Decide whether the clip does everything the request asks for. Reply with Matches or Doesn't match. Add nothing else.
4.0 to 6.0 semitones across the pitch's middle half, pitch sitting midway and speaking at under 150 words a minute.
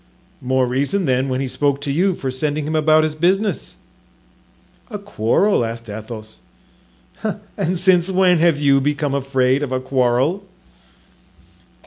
Matches